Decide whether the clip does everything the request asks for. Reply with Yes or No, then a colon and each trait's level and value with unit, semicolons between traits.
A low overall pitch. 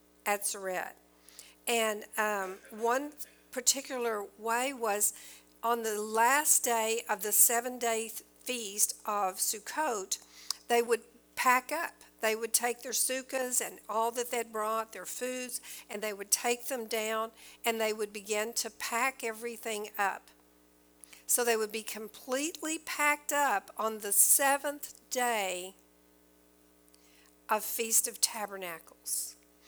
No: high, 220 Hz